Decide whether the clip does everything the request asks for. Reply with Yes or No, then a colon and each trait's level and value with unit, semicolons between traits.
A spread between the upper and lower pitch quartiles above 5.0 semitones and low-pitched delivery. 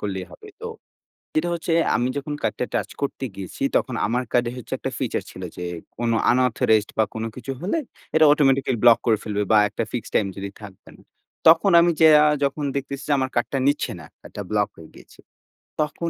Yes: wide, 5.5 semitones; low, 125 Hz